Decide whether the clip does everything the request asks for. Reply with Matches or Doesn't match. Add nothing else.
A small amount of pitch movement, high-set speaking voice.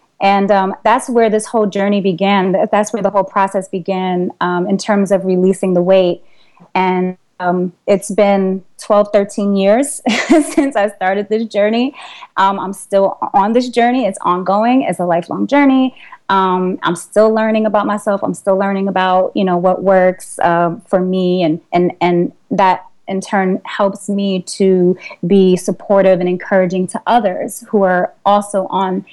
Matches